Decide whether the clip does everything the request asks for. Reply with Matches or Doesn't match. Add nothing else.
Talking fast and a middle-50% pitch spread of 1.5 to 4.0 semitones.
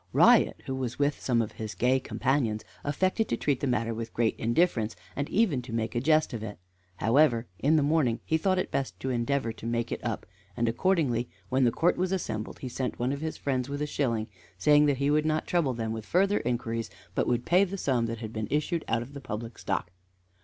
Doesn't match